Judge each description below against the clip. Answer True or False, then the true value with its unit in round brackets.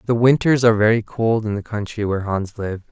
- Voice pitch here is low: True (110 Hz)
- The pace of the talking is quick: True (225 wpm)